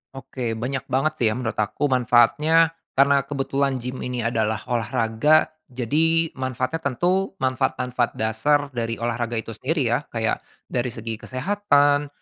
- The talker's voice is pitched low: Yes, low, 130 Hz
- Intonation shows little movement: No, average, 3.7 semitones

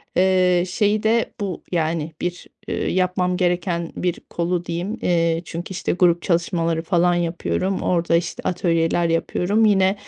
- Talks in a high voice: No, medium, 175 Hz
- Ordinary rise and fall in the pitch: No, narrow, 1.6 semitones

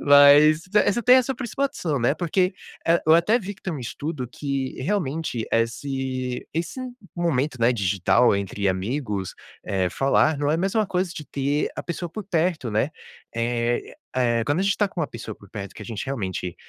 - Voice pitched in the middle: Yes, medium, 145 Hz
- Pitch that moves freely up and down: Yes, wide, 6.7 semitones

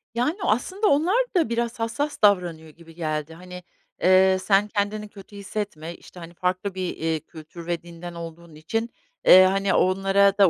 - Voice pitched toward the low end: No, high, 190 Hz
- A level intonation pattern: No, average, 3.8 semitones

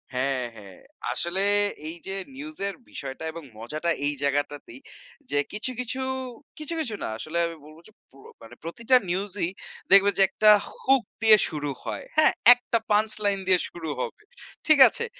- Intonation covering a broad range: Yes, wide, 7.3 semitones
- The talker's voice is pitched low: No, high, 190 Hz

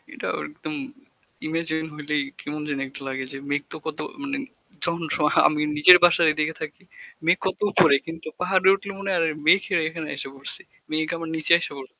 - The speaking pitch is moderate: Yes, medium, 160 Hz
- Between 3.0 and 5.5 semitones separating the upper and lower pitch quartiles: No, narrow, 2.6 semitones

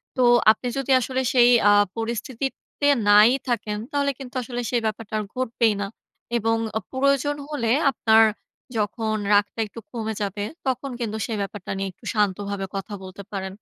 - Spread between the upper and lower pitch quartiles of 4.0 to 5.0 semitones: No, average, 3.5 semitones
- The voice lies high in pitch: Yes, high, 225 Hz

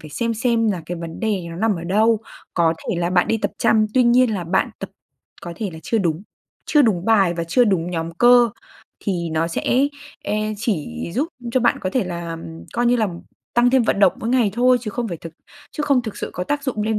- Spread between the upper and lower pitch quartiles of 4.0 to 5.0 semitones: No, wide, 5.6 semitones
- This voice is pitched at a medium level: No, high, 210 Hz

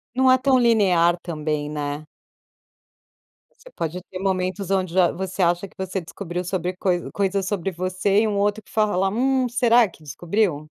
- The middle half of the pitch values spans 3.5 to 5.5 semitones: No, average, 3.1 semitones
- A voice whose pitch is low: No, high, 190 Hz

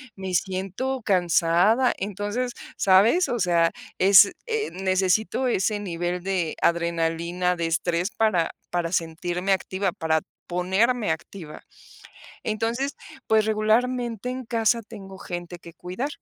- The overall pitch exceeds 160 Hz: Yes, high, 190 Hz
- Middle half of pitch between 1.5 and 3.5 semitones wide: No, average, 4.2 semitones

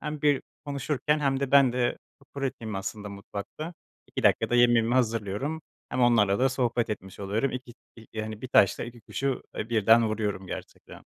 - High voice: No, low, 120 Hz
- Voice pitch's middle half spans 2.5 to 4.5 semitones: Yes, average, 4.1 semitones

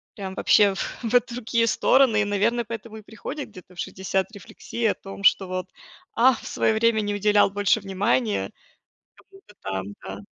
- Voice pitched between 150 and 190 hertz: No, high, 210 Hz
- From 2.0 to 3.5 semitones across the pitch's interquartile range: Yes, average, 2.9 semitones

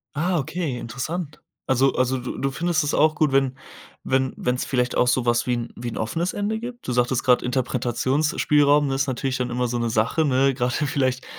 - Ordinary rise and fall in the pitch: Yes, average, 3.2 semitones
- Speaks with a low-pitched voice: Yes, low, 130 Hz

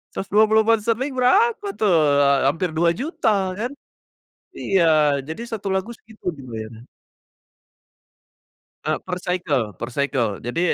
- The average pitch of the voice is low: No, high, 190 Hz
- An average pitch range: No, wide, 8.1 semitones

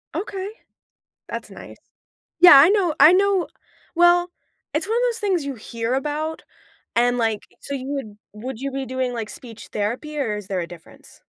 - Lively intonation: Yes, wide, 7.1 semitones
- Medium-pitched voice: No, very high, 275 Hz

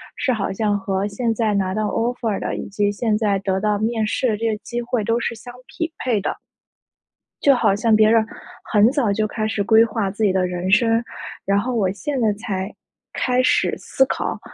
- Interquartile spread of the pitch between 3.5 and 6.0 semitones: No, narrow, 2.6 semitones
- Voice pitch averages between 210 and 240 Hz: Yes, high, 215 Hz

